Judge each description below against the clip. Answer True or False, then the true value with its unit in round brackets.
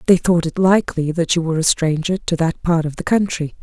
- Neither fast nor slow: False (250 wpm)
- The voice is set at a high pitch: False (170 Hz)